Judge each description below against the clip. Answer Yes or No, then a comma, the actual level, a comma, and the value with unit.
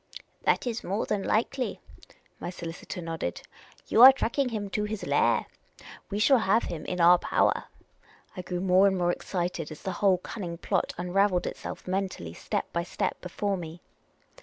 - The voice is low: No, medium, 185 Hz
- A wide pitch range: No, average, 3.1 semitones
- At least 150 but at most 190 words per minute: Yes, average, 185 wpm